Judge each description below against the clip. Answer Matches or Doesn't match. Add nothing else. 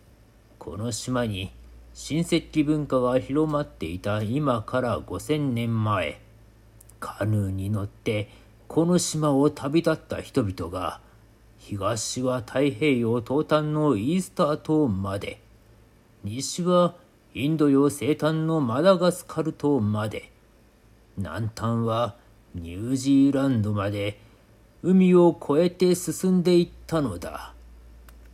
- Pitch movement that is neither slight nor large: Doesn't match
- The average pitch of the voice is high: Doesn't match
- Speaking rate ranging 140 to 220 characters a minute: Matches